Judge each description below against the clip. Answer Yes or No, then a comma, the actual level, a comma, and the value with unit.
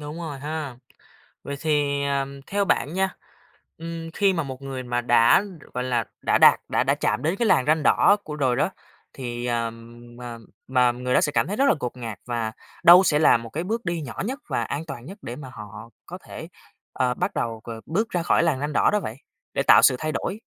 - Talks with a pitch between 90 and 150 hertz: Yes, medium, 140 Hz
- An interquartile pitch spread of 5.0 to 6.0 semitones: Yes, average, 5.3 semitones